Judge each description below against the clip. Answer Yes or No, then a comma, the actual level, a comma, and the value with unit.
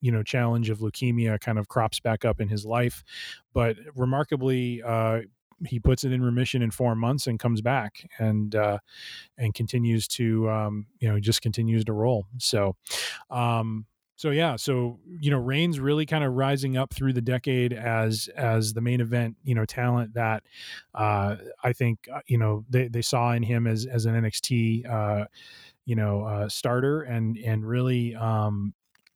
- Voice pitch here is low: Yes, low, 115 Hz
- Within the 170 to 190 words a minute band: Yes, average, 180 wpm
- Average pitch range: No, narrow, 2.2 semitones